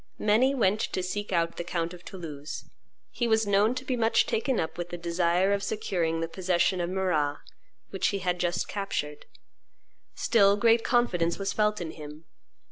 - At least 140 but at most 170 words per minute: No, average, 180 wpm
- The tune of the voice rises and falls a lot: No, average, 3.7 semitones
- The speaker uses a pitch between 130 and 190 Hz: Yes, medium, 185 Hz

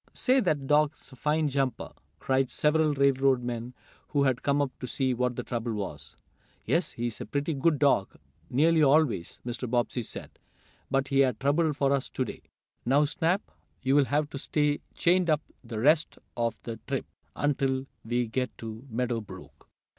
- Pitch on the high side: No, low, 135 Hz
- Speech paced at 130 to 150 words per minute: No, average, 175 wpm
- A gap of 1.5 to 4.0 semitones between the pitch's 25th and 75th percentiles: Yes, average, 3.3 semitones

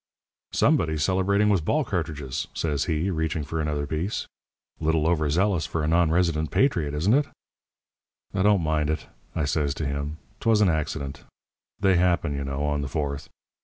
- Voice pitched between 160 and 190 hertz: No, very low, 80 Hz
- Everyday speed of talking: Yes, average, 165 wpm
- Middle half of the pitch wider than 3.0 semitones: Yes, average, 3.5 semitones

